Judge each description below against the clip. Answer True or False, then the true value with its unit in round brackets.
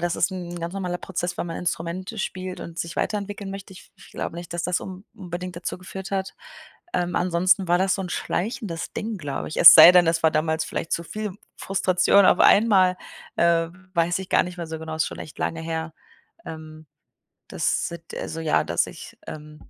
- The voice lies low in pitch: False (175 Hz)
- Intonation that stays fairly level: True (2.2 semitones)